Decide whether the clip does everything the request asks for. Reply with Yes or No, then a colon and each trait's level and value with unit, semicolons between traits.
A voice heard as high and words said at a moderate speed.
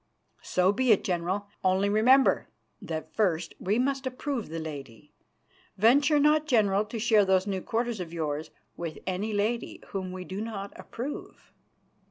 Yes: high, 200 Hz; average, 155 wpm